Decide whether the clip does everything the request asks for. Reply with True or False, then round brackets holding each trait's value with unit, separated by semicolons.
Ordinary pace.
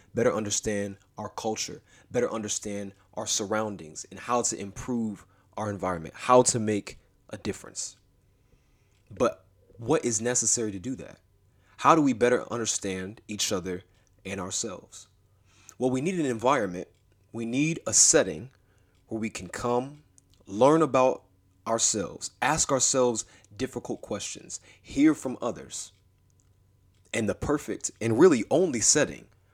False (130 wpm)